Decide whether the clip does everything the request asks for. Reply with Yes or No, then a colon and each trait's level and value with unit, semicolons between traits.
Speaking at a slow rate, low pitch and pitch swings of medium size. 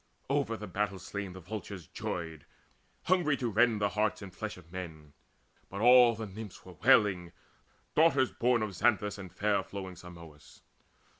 No: average, 160 wpm; low, 100 Hz; average, 4.0 semitones